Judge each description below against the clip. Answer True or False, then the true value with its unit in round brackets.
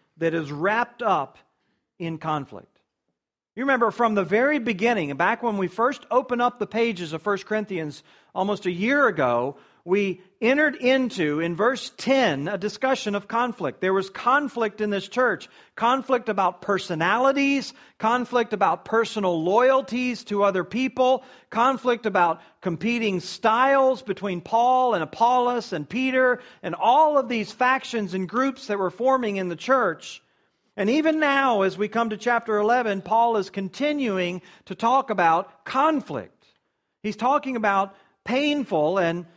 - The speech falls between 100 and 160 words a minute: True (150 wpm)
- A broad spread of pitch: False (5.0 semitones)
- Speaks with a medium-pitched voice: False (220 Hz)